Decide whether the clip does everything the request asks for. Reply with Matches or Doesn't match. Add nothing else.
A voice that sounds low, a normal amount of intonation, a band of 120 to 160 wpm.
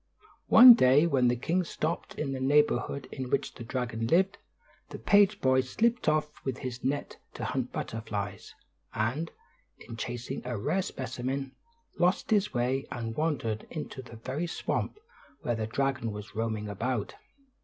Matches